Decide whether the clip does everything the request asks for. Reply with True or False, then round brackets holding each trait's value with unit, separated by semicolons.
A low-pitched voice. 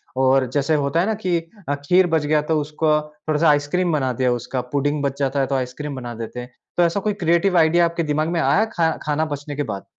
False (150 Hz)